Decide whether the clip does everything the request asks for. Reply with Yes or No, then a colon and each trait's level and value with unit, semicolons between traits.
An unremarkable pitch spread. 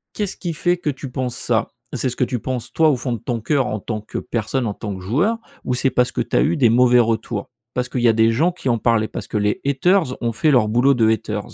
Yes: average, 3.6 semitones